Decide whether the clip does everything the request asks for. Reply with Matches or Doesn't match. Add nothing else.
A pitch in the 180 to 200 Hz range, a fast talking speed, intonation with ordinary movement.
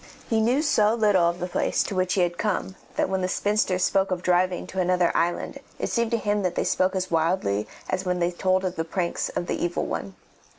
Doesn't match